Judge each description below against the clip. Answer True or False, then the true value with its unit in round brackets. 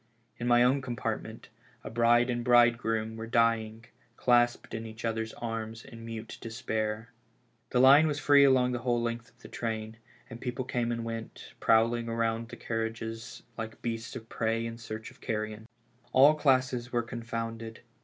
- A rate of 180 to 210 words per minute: False (170 wpm)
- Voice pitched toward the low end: True (115 Hz)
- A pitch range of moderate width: False (1.2 semitones)